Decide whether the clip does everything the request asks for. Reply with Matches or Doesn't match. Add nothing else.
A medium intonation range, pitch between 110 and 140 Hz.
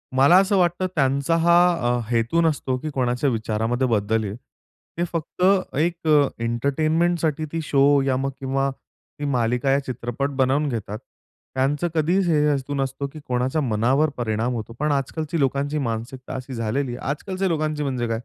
Matches